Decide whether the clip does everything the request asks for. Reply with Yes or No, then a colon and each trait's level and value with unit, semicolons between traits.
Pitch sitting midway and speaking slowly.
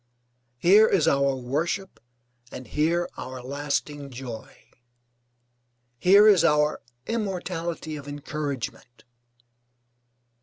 Yes: medium, 150 Hz; slow, 85 wpm